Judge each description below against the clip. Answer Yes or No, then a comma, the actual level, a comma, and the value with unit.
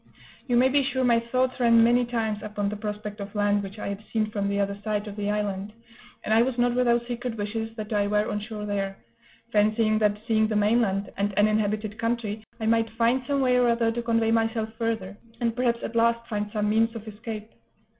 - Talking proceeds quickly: Yes, fast, 225 wpm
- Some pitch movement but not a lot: No, narrow, 2.0 semitones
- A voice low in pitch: No, high, 220 Hz